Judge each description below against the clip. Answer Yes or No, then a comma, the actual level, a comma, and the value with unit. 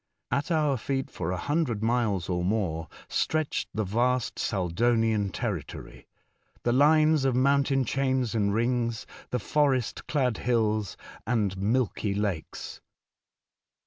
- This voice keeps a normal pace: No, slow, 120 wpm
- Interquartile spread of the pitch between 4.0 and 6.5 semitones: Yes, average, 4.6 semitones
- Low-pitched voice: Yes, low, 120 Hz